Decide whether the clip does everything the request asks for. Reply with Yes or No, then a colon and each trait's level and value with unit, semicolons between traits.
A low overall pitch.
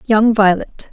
No: high, 215 Hz